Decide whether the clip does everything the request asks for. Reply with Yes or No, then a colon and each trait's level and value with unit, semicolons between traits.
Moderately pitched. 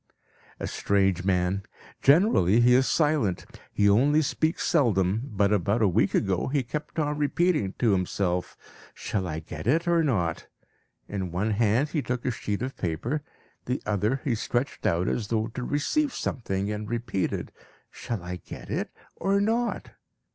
No: low, 110 Hz